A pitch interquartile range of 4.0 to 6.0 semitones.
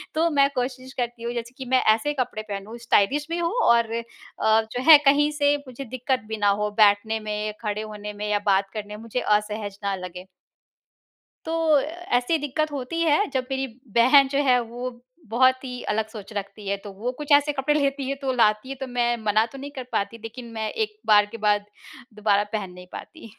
Yes: average, 4.6 semitones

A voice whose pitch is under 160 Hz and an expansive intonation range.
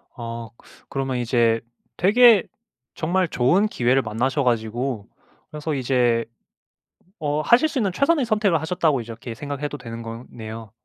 Yes: low, 135 Hz; wide, 6.8 semitones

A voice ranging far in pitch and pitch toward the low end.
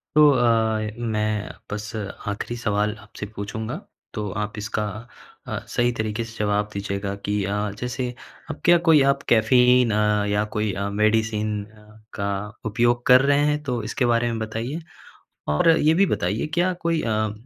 No: average, 2.7 semitones; low, 110 Hz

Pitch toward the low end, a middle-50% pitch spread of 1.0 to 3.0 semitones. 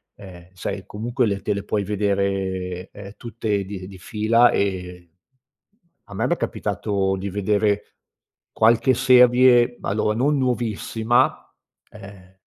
No: low, 105 Hz; average, 3.4 semitones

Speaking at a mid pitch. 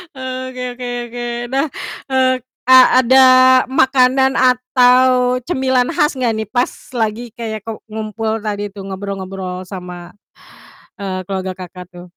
No: high, 240 Hz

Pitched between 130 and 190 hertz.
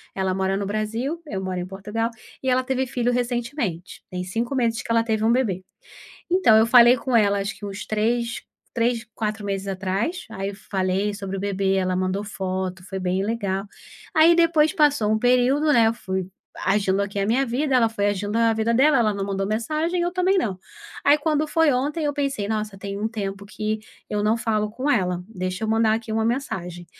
No: high, 220 Hz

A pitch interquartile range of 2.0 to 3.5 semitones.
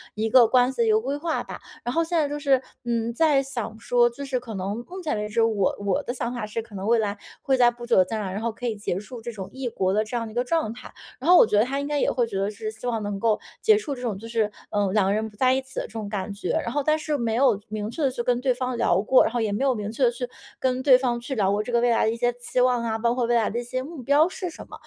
Yes: average, 3.2 semitones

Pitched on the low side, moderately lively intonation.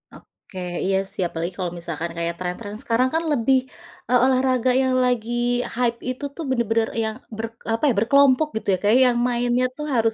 No: high, 235 Hz; average, 3.8 semitones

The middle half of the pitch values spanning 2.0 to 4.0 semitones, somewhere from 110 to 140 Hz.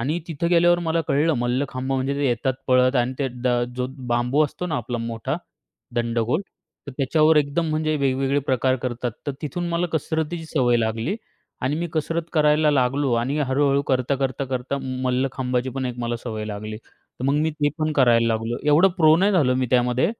Yes: average, 3.7 semitones; low, 135 Hz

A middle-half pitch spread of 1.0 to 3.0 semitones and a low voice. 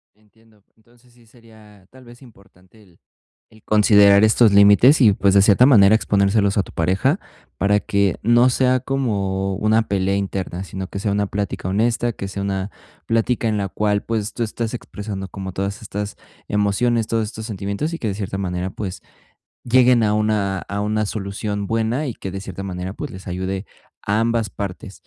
Yes: narrow, 2.5 semitones; low, 105 Hz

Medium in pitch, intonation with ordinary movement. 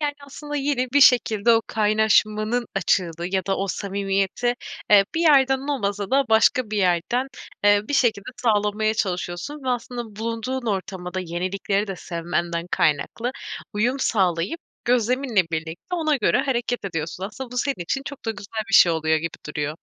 No: high, 215 Hz; average, 5.0 semitones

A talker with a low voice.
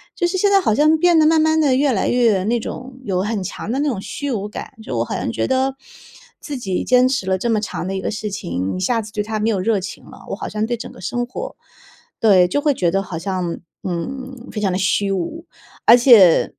No: high, 225 Hz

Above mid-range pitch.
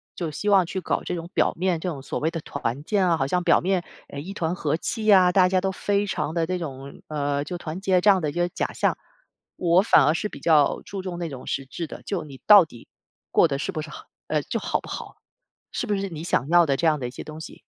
No: medium, 170 Hz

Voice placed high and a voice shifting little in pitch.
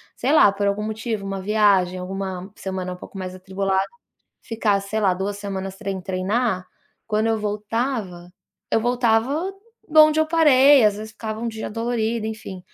No: high, 210 Hz; average, 3.0 semitones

